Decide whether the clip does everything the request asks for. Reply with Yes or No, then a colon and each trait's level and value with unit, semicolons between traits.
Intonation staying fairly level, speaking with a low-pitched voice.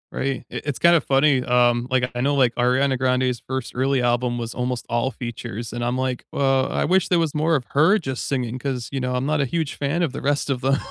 Yes: narrow, 2.3 semitones; low, 130 Hz